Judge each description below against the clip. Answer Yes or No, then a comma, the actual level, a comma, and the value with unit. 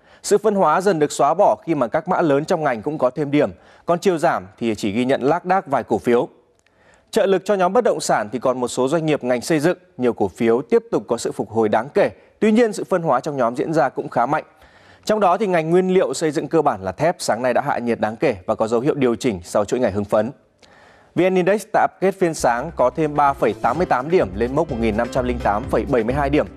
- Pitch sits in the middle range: Yes, medium, 145 Hz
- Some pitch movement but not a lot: No, wide, 7.2 semitones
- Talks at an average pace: No, fast, 255 wpm